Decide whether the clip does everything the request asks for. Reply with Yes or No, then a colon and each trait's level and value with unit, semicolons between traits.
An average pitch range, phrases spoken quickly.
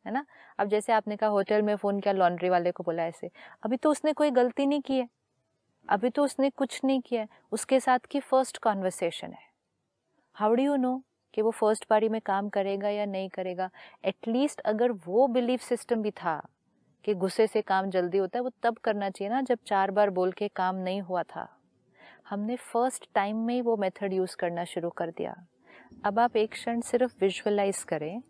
Yes: average, 4.4 semitones; fast, 205 wpm